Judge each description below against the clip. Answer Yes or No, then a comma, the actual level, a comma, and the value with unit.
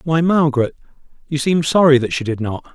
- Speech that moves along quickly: No, average, 195 wpm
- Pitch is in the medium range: Yes, medium, 145 Hz